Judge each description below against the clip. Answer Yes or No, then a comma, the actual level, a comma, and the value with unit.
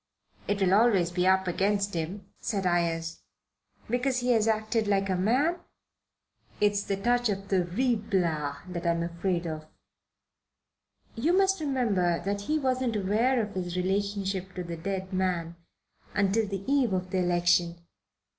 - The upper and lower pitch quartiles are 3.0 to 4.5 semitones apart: Yes, average, 4.0 semitones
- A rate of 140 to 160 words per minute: Yes, average, 150 wpm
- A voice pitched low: No, high, 195 Hz